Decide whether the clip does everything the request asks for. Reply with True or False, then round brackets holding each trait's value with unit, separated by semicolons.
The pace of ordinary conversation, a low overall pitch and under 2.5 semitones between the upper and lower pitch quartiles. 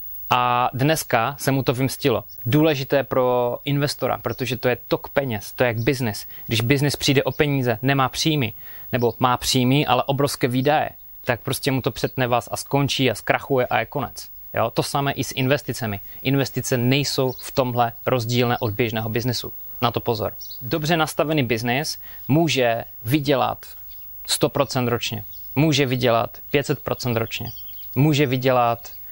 False (150 wpm; 130 Hz; 2.8 semitones)